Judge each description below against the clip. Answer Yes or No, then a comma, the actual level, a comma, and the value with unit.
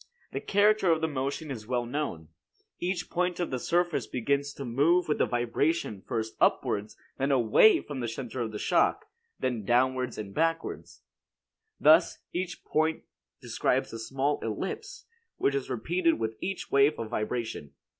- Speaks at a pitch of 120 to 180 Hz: Yes, low, 135 Hz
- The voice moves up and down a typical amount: No, wide, 5.9 semitones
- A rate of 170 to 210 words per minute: No, average, 155 wpm